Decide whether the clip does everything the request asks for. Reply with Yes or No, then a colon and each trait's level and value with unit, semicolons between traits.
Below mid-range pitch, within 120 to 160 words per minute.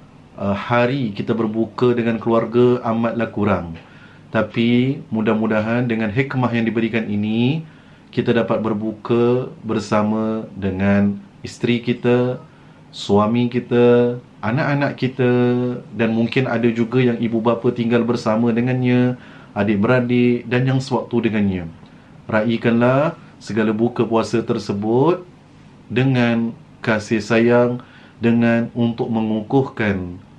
No: low, 120 Hz; average, 105 wpm